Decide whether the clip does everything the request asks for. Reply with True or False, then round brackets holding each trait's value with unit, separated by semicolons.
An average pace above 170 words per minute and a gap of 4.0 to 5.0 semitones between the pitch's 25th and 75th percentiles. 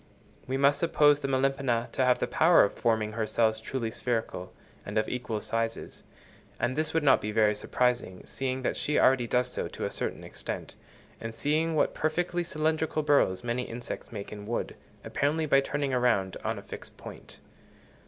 True (185 wpm; 4.4 semitones)